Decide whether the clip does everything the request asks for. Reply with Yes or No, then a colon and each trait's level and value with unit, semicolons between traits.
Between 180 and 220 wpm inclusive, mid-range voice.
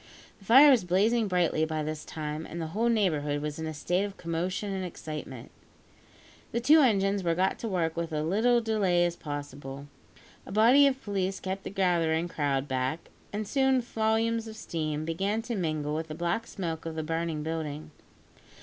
Yes: average, 185 wpm; medium, 175 Hz